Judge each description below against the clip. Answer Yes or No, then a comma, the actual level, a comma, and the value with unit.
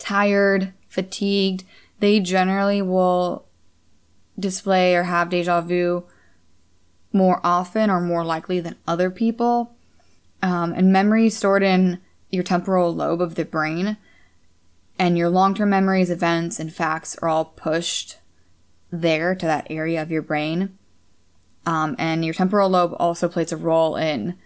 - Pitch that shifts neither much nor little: Yes, average, 3.1 semitones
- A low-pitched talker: No, medium, 175 Hz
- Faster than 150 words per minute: No, slow, 135 wpm